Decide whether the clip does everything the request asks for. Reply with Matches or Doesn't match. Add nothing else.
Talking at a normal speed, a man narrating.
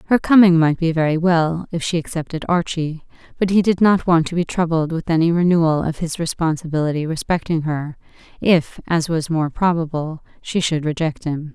Doesn't match